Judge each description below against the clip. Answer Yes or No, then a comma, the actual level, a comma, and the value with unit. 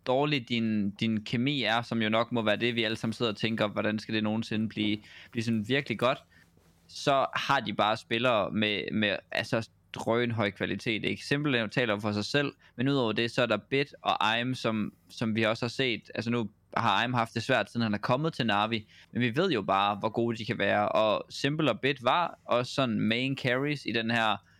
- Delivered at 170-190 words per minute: No, fast, 225 wpm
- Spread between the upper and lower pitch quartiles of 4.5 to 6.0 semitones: No, narrow, 2.5 semitones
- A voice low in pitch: Yes, low, 115 Hz